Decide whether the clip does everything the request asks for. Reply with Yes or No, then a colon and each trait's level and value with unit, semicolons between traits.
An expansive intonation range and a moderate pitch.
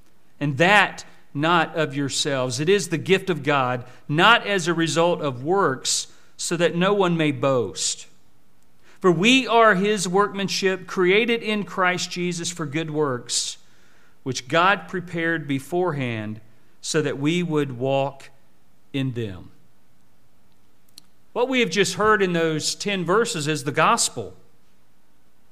Yes: wide, 6.2 semitones; medium, 160 Hz